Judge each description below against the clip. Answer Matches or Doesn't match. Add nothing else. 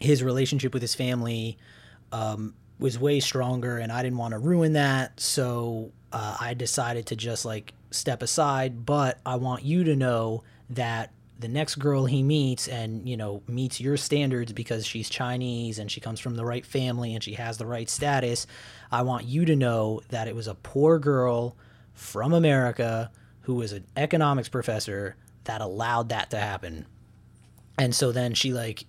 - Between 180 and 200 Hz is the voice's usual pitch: Doesn't match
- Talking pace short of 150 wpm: Doesn't match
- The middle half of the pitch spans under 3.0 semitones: Matches